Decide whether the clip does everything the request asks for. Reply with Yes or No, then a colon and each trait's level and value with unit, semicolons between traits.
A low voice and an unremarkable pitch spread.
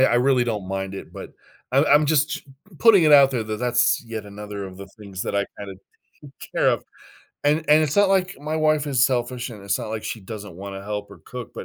No: low, 120 Hz; wide, 6.4 semitones